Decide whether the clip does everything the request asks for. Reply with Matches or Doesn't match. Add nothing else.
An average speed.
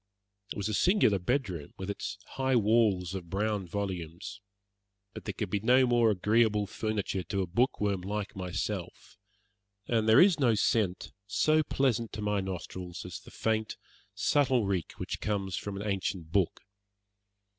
Matches